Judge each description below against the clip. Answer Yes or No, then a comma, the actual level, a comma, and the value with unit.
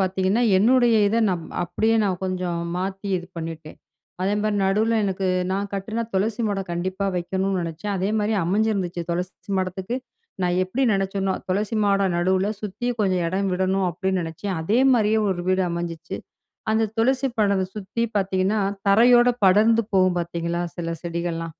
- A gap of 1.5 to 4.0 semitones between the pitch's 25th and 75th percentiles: Yes, average, 2.7 semitones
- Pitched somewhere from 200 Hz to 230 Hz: No, high, 190 Hz